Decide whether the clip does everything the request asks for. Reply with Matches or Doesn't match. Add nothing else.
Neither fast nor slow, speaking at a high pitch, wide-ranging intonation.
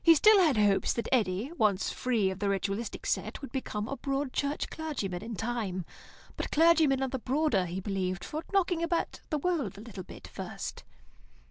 Matches